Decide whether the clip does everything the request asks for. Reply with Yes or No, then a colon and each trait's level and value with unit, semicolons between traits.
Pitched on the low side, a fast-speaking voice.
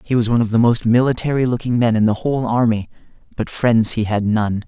Yes: low, 115 Hz; fast, 230 wpm